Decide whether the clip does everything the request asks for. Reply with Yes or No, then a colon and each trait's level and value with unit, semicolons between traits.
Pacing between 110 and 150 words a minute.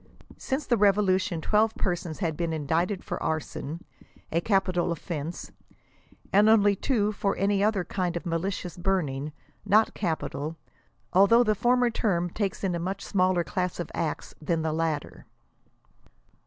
Yes: average, 145 wpm